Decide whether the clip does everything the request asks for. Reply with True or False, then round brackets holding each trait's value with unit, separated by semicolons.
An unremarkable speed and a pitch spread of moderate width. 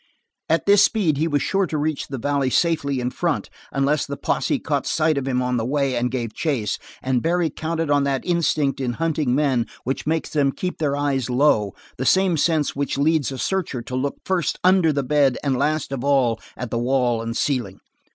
False (210 wpm; 3.7 semitones)